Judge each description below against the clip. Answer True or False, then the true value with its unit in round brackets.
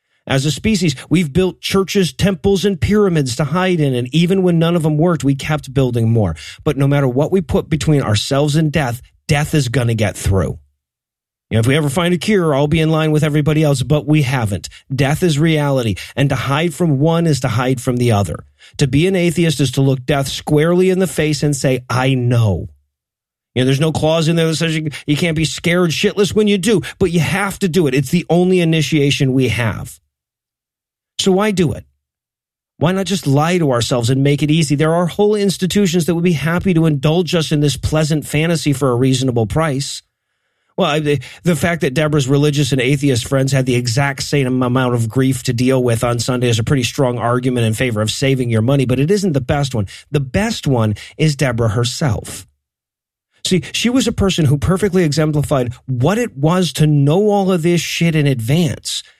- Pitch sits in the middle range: True (150 Hz)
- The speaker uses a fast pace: True (215 wpm)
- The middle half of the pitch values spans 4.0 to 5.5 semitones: True (4.7 semitones)